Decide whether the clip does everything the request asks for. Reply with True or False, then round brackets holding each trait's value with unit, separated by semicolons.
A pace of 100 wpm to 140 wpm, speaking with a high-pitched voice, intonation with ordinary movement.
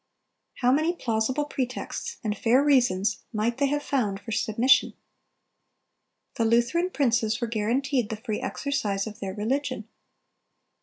True (135 wpm; 235 Hz; 4.1 semitones)